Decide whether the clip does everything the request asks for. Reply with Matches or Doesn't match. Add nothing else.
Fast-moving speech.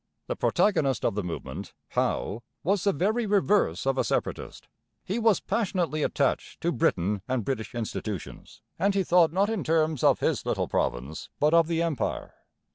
Doesn't match